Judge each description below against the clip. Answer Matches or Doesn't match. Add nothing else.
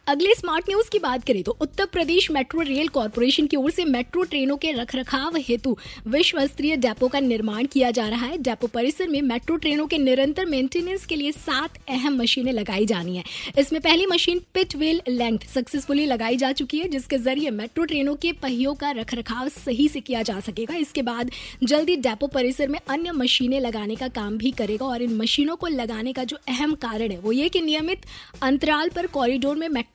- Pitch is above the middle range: Matches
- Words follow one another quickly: Matches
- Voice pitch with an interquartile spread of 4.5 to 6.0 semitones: Doesn't match